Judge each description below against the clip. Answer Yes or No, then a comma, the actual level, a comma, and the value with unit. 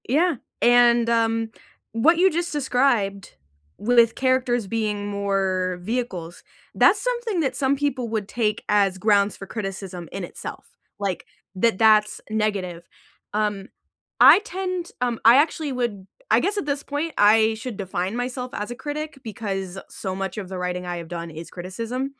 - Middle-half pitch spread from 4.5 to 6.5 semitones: Yes, average, 5.0 semitones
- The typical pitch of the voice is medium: No, high, 220 Hz